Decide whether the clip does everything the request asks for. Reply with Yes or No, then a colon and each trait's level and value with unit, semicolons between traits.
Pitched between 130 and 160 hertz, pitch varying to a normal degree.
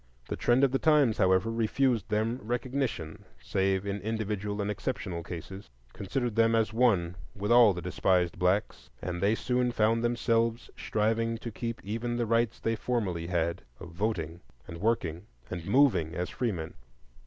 No: low, 110 Hz; average, 4.3 semitones